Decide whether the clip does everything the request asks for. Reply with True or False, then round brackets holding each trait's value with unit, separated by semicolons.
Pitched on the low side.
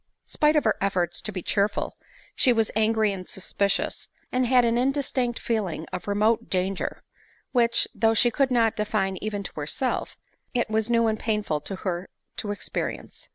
False (215 Hz)